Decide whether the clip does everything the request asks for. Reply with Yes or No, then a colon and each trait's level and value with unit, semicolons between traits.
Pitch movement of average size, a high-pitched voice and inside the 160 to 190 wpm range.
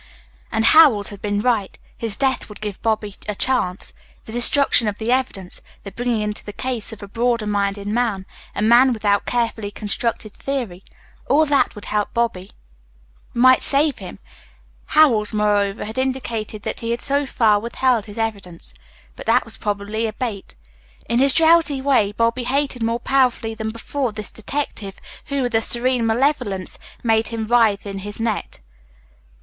Yes: average, 3.4 semitones; high, 225 Hz; average, 170 wpm